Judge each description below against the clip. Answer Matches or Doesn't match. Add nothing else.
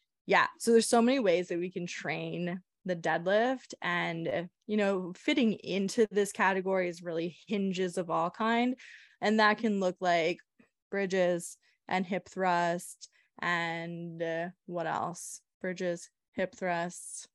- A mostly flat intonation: Doesn't match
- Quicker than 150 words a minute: Doesn't match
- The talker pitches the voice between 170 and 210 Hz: Matches